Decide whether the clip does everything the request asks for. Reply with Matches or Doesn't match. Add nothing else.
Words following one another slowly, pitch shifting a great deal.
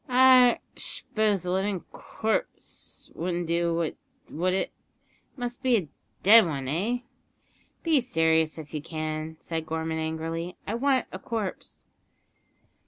Matches